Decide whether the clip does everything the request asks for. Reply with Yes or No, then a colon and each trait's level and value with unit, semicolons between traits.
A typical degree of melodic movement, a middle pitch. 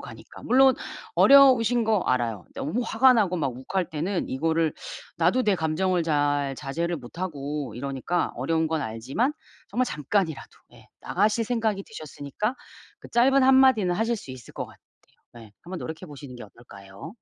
No: wide, 7.8 semitones; medium, 165 Hz